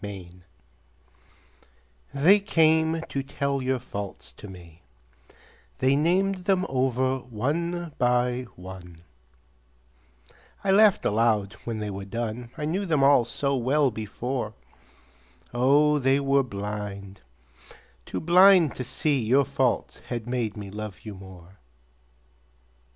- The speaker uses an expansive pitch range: Yes, wide, 5.9 semitones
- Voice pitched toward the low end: Yes, low, 125 Hz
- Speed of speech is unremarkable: No, slow, 120 wpm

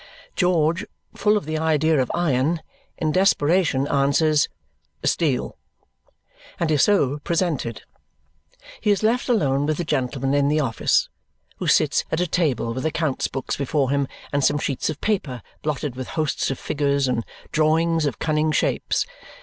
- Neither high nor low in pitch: Yes, medium, 150 Hz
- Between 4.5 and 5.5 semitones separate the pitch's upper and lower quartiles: No, average, 3.2 semitones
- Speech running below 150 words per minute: No, average, 155 wpm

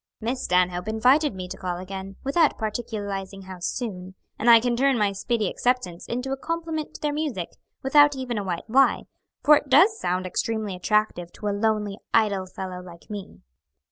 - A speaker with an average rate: Yes, average, 180 wpm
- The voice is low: No, high, 215 Hz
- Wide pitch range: Yes, wide, 5.7 semitones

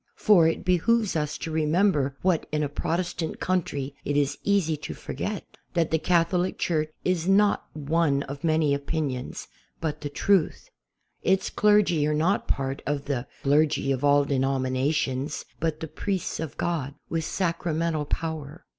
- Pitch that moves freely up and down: No, average, 3.4 semitones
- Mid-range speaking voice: Yes, medium, 155 Hz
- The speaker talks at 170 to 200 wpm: No, average, 155 wpm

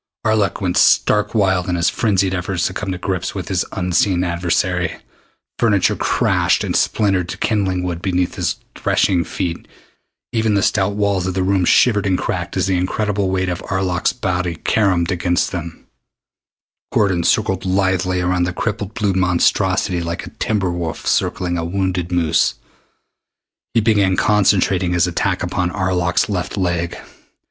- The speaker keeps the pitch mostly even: Yes, narrow, 1.9 semitones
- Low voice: Yes, very low, 95 Hz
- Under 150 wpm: No, average, 155 wpm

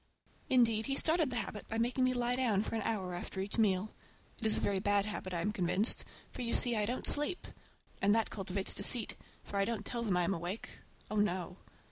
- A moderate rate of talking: No, fast, 215 wpm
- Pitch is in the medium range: No, high, 215 Hz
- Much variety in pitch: No, average, 3.5 semitones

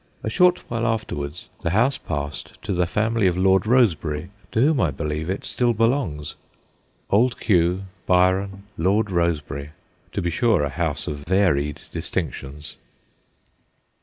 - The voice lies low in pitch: Yes, very low, 90 Hz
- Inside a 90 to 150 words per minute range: Yes, average, 145 wpm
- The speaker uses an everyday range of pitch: No, wide, 6.5 semitones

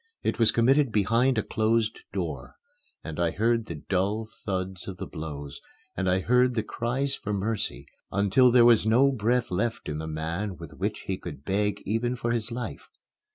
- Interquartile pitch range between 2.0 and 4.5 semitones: Yes, average, 4.2 semitones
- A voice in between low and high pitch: No, low, 110 Hz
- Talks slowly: No, average, 185 wpm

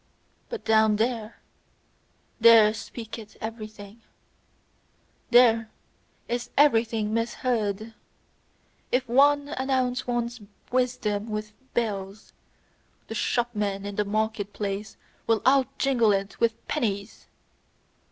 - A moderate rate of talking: No, slow, 95 wpm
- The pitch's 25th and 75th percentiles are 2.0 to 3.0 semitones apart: Yes, narrow, 2.4 semitones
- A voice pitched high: Yes, high, 225 Hz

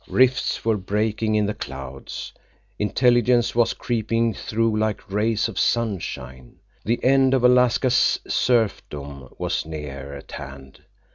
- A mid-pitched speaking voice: No, low, 110 Hz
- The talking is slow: Yes, slow, 125 wpm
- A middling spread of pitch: No, wide, 8.4 semitones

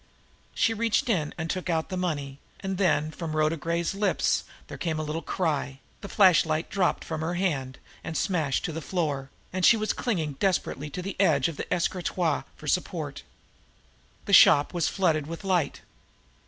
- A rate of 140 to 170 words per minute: No, average, 180 wpm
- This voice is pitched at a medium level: Yes, medium, 165 Hz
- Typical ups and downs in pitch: Yes, average, 3.3 semitones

